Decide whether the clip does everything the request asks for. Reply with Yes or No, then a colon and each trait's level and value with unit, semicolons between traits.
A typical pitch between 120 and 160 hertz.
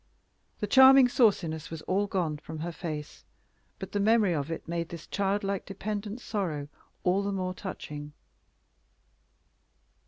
No: high, 190 Hz